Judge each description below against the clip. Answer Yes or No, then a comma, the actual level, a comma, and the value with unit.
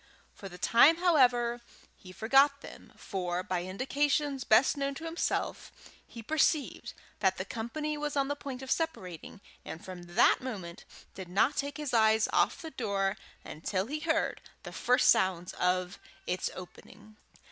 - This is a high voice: Yes, high, 235 Hz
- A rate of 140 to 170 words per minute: Yes, average, 160 wpm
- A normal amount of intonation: No, wide, 7.3 semitones